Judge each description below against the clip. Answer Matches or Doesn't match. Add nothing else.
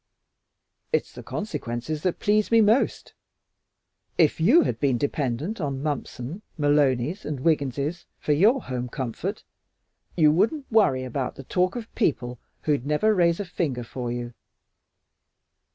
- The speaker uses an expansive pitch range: Matches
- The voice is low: Doesn't match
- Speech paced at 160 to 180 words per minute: Doesn't match